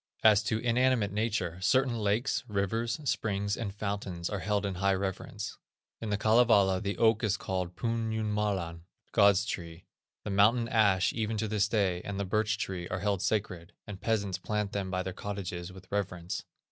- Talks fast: No, average, 175 wpm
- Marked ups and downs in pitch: No, narrow, 2.6 semitones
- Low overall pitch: Yes, low, 100 Hz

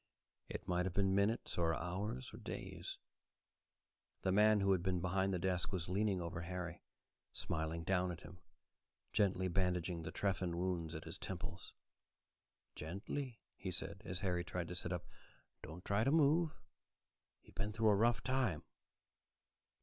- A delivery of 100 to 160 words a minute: Yes, average, 155 wpm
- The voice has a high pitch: No, very low, 90 Hz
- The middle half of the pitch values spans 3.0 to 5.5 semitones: No, narrow, 2.5 semitones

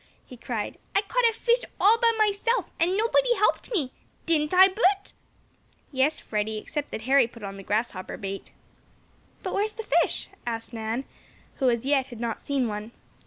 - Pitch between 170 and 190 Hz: No, very high, 275 Hz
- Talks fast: No, average, 175 wpm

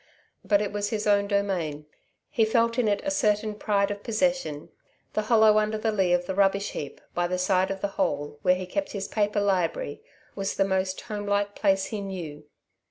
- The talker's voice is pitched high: Yes, high, 200 Hz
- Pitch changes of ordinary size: No, narrow, 2.3 semitones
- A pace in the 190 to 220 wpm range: Yes, average, 200 wpm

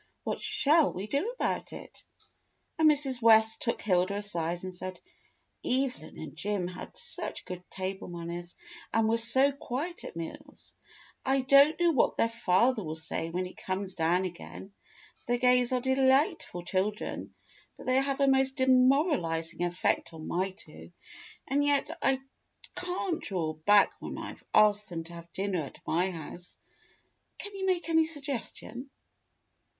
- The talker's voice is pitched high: Yes, high, 220 Hz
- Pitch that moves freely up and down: Yes, wide, 7.2 semitones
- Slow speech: No, average, 155 wpm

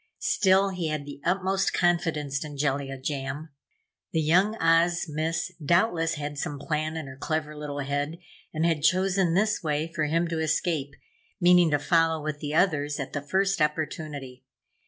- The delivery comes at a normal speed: Yes, average, 165 wpm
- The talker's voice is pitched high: No, medium, 155 Hz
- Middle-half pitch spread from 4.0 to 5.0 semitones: No, average, 2.9 semitones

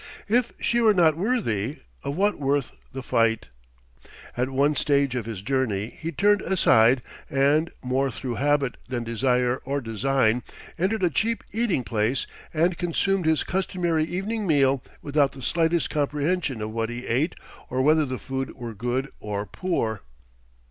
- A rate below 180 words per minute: Yes, average, 155 wpm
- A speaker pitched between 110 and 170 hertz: Yes, medium, 140 Hz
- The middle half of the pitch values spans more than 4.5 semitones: Yes, wide, 5.6 semitones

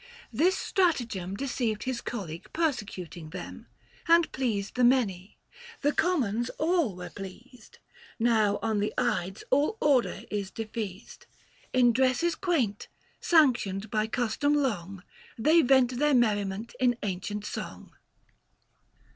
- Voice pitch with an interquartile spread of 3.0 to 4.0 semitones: No, average, 5.3 semitones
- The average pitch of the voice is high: Yes, high, 235 Hz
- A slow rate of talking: Yes, slow, 125 wpm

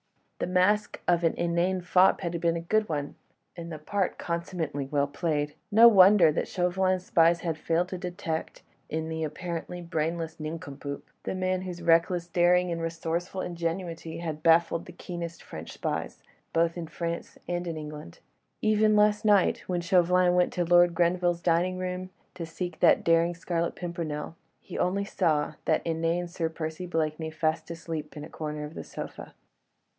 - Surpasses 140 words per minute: Yes, average, 170 wpm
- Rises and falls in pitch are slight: Yes, narrow, 1.8 semitones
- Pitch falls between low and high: Yes, medium, 170 Hz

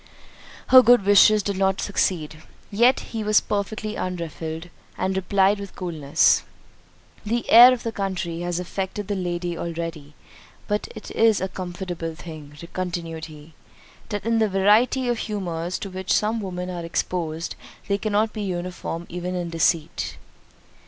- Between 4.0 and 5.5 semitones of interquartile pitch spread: No, average, 3.5 semitones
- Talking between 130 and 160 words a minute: Yes, average, 145 wpm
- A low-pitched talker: No, medium, 185 Hz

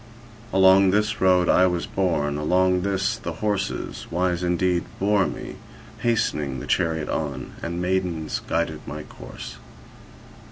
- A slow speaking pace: Yes, slow, 130 wpm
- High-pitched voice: No, very low, 90 Hz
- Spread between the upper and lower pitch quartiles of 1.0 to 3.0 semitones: Yes, average, 2.7 semitones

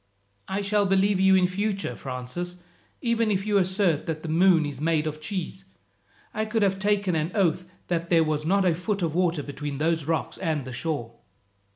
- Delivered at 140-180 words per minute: No, average, 195 wpm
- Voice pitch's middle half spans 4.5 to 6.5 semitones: No, average, 4.0 semitones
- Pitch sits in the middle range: Yes, medium, 175 Hz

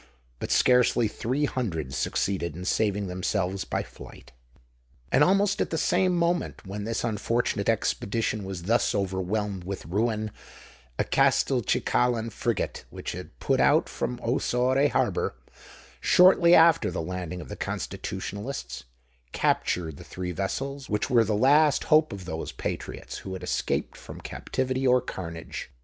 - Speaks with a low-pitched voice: Yes, low, 105 Hz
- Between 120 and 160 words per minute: Yes, average, 140 wpm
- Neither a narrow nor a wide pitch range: No, wide, 5.9 semitones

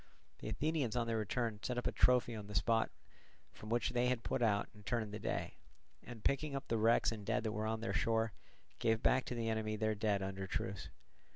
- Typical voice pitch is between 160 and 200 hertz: No, low, 110 Hz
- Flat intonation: Yes, narrow, 2.1 semitones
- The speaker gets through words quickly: Yes, fast, 225 wpm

